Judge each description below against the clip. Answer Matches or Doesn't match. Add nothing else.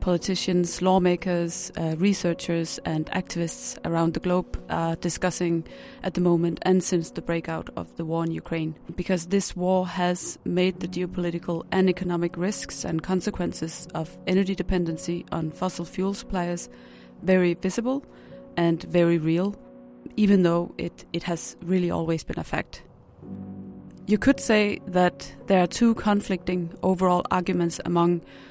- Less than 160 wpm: Matches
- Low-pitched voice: Doesn't match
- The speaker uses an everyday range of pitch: Doesn't match